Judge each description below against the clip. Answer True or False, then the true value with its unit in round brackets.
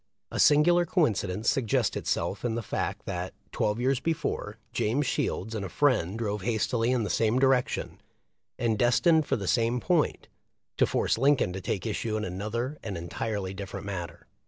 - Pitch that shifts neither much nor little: True (4.4 semitones)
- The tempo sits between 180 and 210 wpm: False (170 wpm)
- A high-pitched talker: False (115 Hz)